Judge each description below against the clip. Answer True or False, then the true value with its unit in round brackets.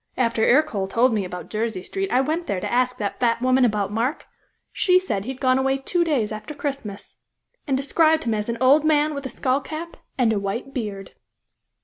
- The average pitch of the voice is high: True (255 Hz)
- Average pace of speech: False (215 wpm)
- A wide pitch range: False (4.9 semitones)